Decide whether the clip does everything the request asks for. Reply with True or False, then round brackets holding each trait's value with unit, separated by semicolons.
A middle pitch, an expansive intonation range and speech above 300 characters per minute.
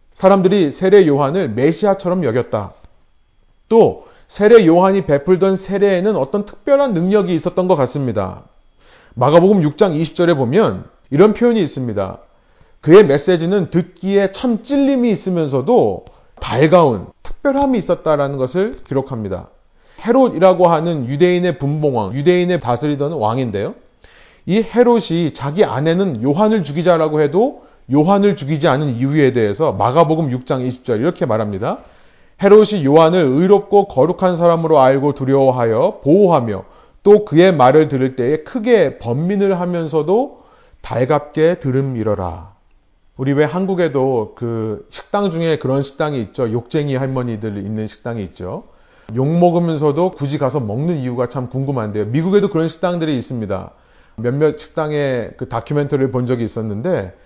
True (155 Hz; 6.3 semitones; 330 characters per minute)